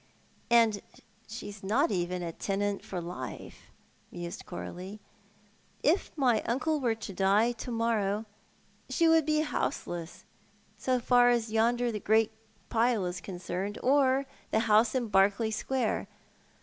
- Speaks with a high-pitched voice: Yes, high, 220 Hz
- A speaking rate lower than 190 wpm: Yes, average, 150 wpm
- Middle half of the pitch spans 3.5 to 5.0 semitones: Yes, average, 3.8 semitones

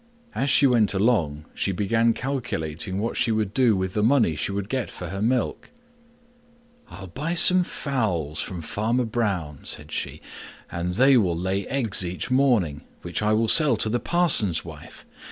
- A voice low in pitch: Yes, low, 105 Hz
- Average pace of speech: Yes, average, 170 wpm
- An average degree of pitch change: No, wide, 5.7 semitones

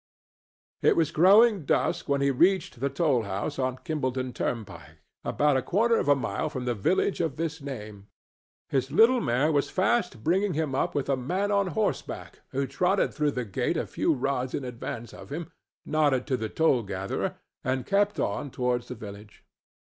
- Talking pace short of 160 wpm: No, average, 185 wpm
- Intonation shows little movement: No, average, 5.0 semitones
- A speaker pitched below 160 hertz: Yes, medium, 140 Hz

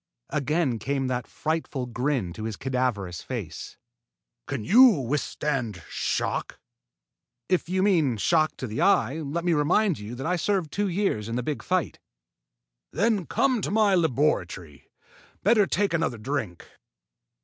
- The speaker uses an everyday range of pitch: No, wide, 7.0 semitones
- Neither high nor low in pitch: Yes, medium, 145 Hz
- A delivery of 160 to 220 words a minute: No, average, 145 wpm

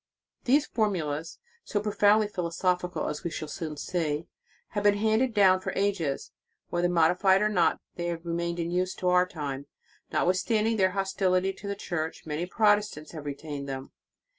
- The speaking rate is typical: Yes, average, 175 wpm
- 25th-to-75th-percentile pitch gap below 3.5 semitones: No, average, 3.8 semitones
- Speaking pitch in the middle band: Yes, medium, 180 Hz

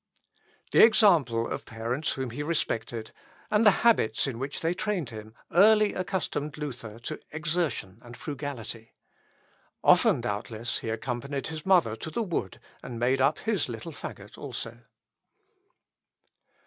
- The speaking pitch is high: No, medium, 140 Hz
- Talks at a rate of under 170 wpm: Yes, slow, 135 wpm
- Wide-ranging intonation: Yes, wide, 6.8 semitones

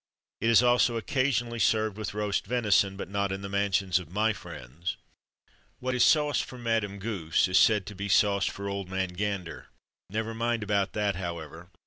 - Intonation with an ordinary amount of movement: Yes, average, 3.1 semitones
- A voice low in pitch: Yes, low, 100 Hz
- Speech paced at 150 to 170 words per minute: No, average, 180 wpm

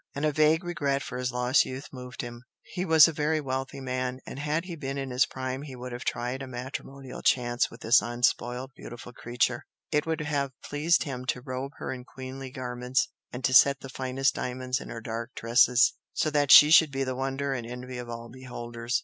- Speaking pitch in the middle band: No, low, 130 Hz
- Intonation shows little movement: Yes, narrow, 2.1 semitones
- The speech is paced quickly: Yes, fast, 215 wpm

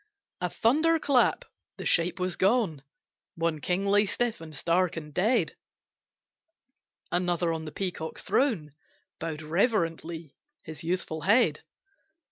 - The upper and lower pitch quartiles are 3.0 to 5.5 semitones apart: Yes, average, 4.5 semitones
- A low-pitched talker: No, medium, 175 Hz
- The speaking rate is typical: No, slow, 120 wpm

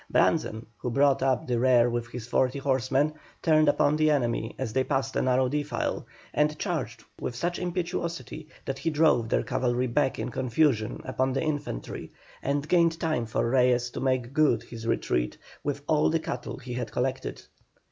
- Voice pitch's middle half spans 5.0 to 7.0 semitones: No, average, 3.6 semitones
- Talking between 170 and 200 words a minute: Yes, average, 180 wpm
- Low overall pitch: Yes, low, 130 Hz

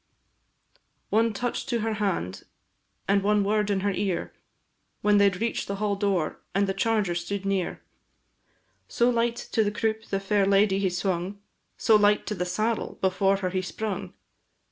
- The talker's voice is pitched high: Yes, high, 200 Hz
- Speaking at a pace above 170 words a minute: No, average, 165 wpm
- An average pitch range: No, narrow, 1.9 semitones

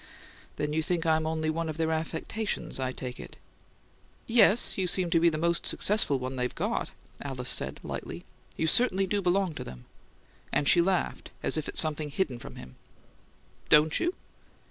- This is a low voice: No, medium, 160 Hz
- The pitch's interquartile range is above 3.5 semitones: Yes, average, 3.9 semitones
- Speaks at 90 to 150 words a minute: No, average, 180 wpm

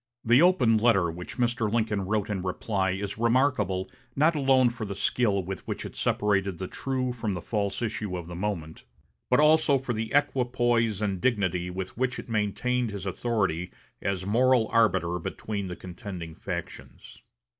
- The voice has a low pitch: Yes, low, 105 Hz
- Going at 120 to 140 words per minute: No, average, 165 wpm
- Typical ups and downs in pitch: Yes, average, 4.4 semitones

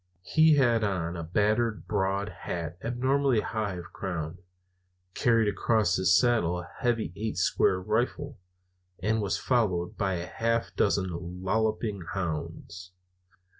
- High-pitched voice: No, low, 105 Hz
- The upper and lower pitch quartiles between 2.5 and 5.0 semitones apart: Yes, average, 4.2 semitones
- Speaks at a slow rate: Yes, slow, 130 wpm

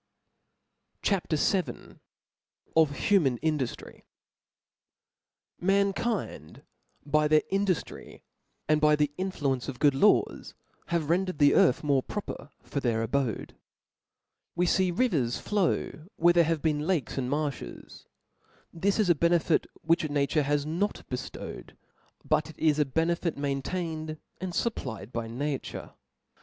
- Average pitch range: Yes, average, 3.8 semitones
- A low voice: No, medium, 155 Hz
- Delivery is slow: Yes, slow, 125 wpm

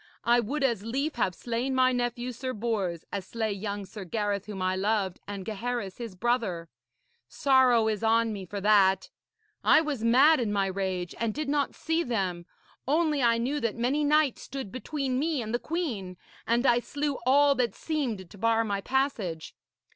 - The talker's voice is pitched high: Yes, high, 230 Hz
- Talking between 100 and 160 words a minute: No, average, 185 wpm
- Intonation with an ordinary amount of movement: Yes, average, 4.9 semitones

